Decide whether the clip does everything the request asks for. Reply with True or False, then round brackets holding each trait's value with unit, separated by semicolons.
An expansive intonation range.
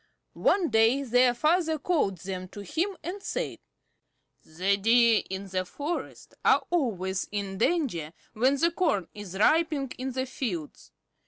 True (8.4 semitones)